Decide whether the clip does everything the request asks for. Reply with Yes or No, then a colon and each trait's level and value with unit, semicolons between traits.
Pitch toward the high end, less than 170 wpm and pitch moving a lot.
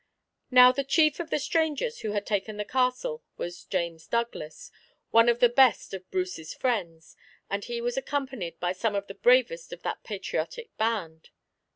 No: high, 235 Hz; average, 175 wpm; wide, 6.0 semitones